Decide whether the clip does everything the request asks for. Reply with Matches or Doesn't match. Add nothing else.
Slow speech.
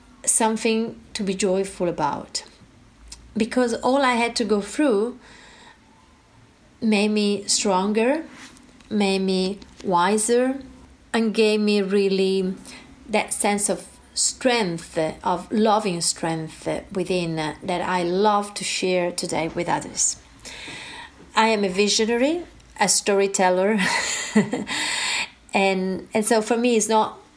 Matches